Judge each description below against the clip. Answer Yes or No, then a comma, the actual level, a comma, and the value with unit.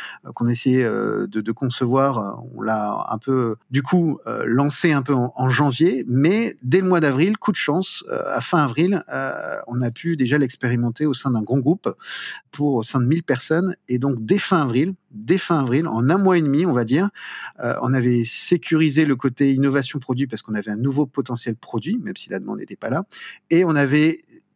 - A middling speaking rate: Yes, average, 205 wpm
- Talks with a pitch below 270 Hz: Yes, medium, 140 Hz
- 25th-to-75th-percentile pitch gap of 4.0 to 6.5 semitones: Yes, average, 4.8 semitones